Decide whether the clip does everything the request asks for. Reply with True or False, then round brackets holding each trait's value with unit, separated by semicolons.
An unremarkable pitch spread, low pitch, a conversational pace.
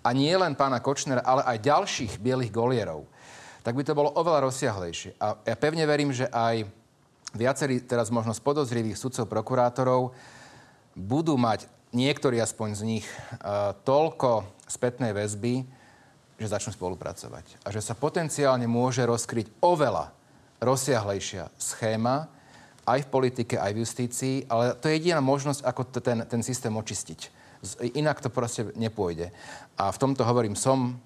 True (3.1 semitones; 125 Hz; 145 wpm)